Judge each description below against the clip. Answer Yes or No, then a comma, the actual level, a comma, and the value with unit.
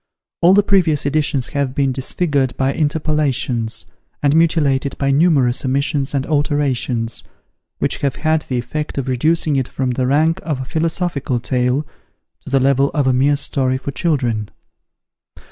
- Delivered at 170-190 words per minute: No, average, 155 wpm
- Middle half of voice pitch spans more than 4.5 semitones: No, average, 2.8 semitones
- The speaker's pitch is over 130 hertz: Yes, medium, 140 Hz